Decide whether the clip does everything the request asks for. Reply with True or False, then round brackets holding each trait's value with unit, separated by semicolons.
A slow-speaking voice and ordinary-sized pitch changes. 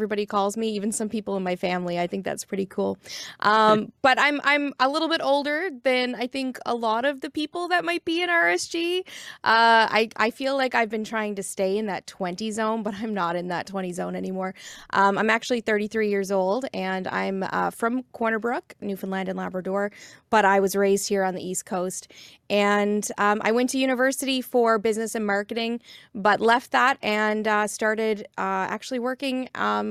False (205 wpm; 4.1 semitones)